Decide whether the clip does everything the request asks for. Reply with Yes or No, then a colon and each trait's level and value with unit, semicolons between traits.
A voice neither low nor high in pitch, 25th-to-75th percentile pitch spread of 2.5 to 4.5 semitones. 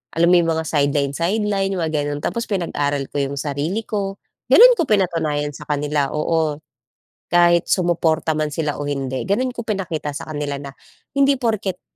No: medium, 160 Hz; average, 5.0 semitones